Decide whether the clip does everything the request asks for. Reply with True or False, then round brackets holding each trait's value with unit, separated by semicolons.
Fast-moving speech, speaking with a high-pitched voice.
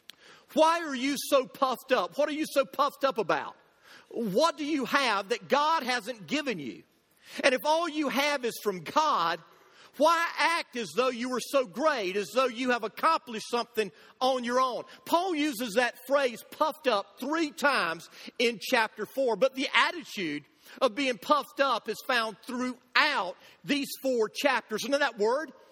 False (175 wpm; 265 Hz)